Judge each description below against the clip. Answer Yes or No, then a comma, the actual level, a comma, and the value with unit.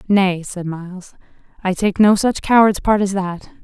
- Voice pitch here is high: Yes, high, 195 Hz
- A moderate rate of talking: Yes, average, 180 wpm